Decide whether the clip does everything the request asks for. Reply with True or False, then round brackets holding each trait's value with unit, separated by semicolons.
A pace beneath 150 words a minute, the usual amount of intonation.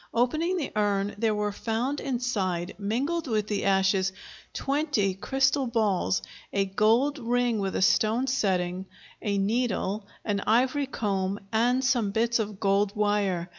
True (140 wpm; 4.0 semitones)